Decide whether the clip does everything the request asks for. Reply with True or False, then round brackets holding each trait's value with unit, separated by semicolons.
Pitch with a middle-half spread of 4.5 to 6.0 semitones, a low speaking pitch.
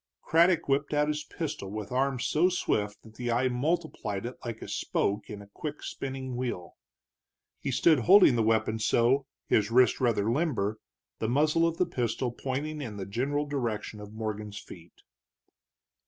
True (5.2 semitones; 125 Hz)